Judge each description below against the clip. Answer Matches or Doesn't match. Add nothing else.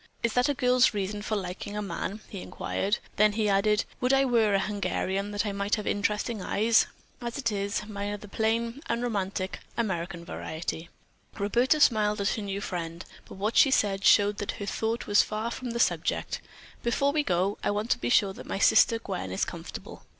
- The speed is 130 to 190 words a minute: Doesn't match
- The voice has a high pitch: Matches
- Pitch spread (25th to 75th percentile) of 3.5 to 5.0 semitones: Doesn't match